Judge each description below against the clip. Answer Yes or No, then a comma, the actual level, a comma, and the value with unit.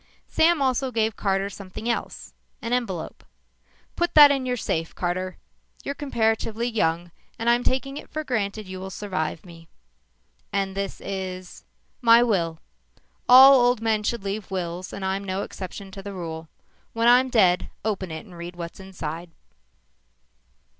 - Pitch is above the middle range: Yes, high, 200 Hz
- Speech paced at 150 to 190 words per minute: Yes, average, 155 wpm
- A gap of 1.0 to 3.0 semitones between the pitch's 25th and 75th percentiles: No, average, 4.6 semitones